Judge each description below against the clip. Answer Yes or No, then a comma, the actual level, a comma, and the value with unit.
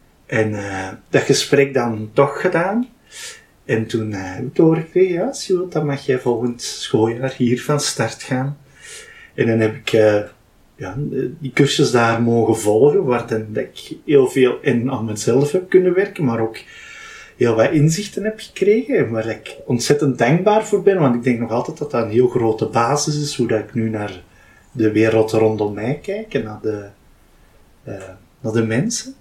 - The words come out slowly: No, average, 175 wpm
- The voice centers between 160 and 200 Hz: No, low, 125 Hz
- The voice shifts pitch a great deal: Yes, wide, 6.4 semitones